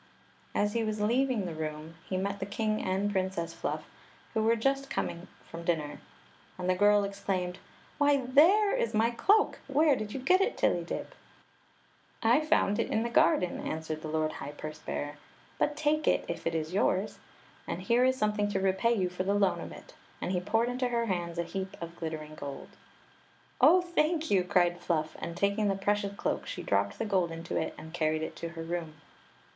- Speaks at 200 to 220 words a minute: Yes, fast, 205 wpm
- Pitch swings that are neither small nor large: No, wide, 5.7 semitones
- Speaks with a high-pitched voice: Yes, high, 195 Hz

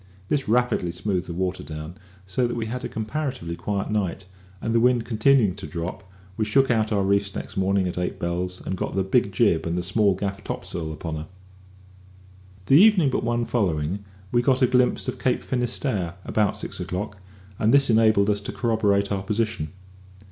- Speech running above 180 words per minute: Yes, average, 190 wpm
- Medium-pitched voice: No, low, 105 Hz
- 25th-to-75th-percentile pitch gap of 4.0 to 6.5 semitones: Yes, average, 4.5 semitones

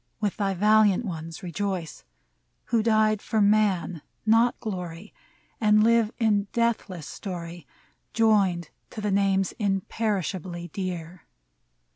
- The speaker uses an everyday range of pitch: Yes, average, 3.3 semitones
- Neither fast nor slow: No, slow, 110 wpm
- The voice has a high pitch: Yes, high, 200 Hz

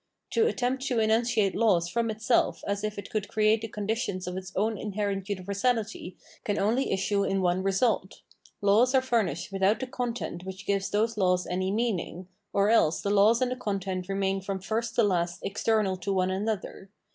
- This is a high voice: Yes, high, 200 Hz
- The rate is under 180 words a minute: No, average, 185 wpm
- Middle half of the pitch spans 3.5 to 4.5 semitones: No, average, 2.9 semitones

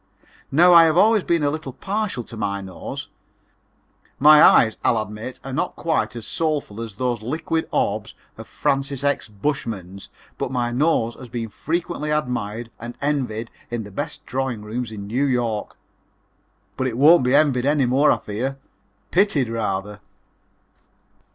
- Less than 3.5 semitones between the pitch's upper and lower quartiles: No, average, 5.1 semitones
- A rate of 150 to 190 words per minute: Yes, average, 155 wpm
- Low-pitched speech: Yes, low, 125 Hz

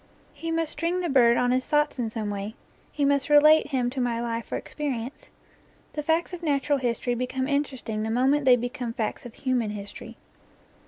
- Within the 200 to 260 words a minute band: Yes, fast, 205 wpm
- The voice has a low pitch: No, very high, 260 Hz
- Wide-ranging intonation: No, average, 3.8 semitones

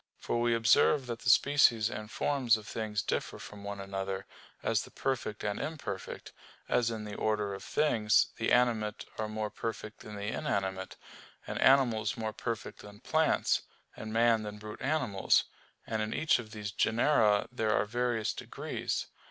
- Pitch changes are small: Yes, narrow, 2.3 semitones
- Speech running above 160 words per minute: Yes, average, 170 wpm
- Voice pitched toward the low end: Yes, low, 110 Hz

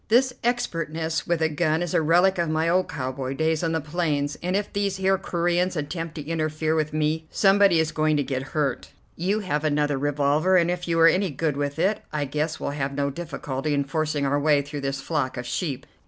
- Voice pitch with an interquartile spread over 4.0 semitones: No, average, 3.2 semitones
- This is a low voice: No, medium, 155 Hz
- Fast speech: Yes, fast, 220 wpm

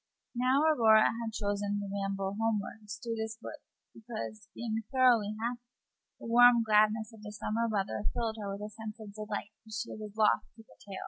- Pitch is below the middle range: No, high, 220 Hz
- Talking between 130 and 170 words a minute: No, average, 185 wpm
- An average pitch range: No, narrow, 1.8 semitones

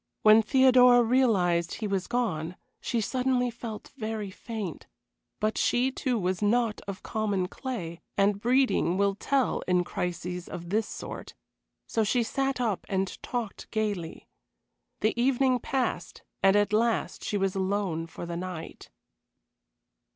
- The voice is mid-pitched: No, high, 215 Hz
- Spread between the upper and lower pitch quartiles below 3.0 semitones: No, average, 4.7 semitones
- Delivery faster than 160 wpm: No, average, 140 wpm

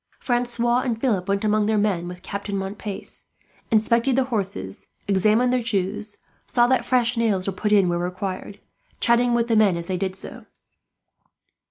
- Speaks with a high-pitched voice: Yes, high, 210 Hz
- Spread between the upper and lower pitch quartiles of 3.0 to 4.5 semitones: Yes, average, 3.7 semitones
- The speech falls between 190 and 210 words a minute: No, average, 170 wpm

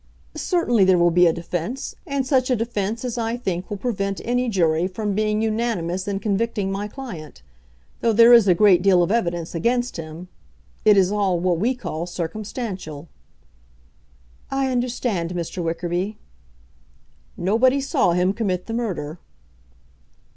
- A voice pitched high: Yes, high, 200 Hz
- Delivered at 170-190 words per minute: No, average, 150 wpm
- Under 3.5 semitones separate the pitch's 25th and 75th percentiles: No, average, 4.9 semitones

